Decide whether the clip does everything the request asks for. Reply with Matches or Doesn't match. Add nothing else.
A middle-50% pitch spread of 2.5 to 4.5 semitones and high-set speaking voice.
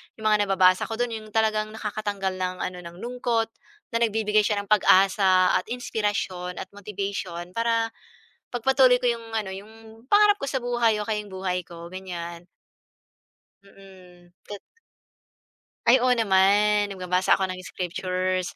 Matches